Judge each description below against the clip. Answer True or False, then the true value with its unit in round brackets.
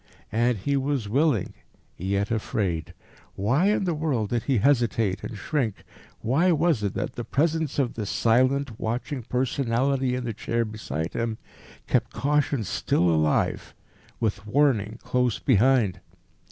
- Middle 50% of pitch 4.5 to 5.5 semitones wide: True (4.8 semitones)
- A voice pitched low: True (120 Hz)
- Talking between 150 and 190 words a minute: False (140 wpm)